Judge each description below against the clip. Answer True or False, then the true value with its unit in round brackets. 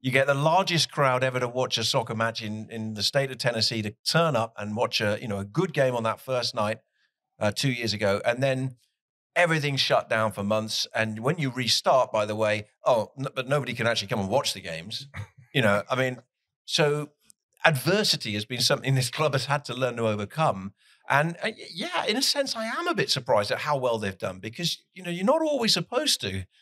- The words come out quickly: True (230 wpm)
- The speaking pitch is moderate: False (130 Hz)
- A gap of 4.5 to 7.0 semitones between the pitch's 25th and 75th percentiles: True (5.2 semitones)